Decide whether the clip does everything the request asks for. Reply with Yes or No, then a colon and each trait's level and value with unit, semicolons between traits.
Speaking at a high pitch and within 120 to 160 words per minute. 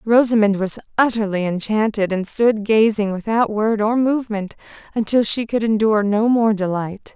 Yes: high, 215 Hz; average, 150 wpm